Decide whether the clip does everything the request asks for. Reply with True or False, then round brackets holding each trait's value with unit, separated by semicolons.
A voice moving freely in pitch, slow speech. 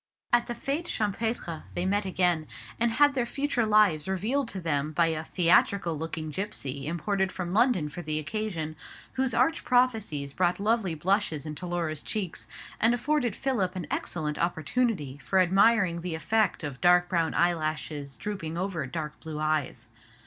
False (5.7 semitones; 160 wpm)